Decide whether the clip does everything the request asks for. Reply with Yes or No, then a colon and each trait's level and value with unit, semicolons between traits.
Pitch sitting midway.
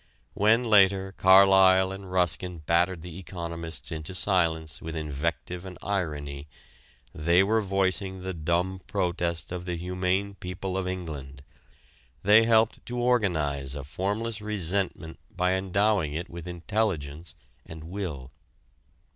No: very low, 90 Hz